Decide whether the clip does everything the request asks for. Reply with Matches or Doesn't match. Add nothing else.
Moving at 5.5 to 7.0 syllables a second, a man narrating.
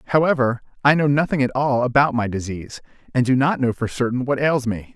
Matches